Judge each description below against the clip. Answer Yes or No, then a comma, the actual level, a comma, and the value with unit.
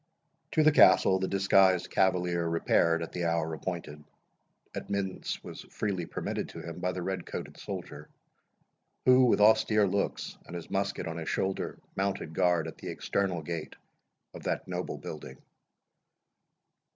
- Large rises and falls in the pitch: No, average, 2.9 semitones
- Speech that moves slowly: No, average, 150 wpm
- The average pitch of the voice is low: Yes, very low, 90 Hz